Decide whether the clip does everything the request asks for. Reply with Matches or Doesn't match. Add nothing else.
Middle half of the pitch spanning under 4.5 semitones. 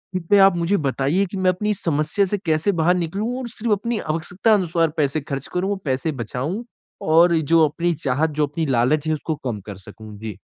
Doesn't match